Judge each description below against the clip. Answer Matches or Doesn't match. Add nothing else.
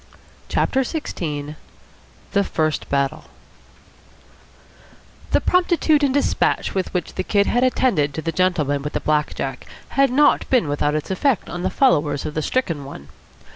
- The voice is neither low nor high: Matches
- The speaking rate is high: Doesn't match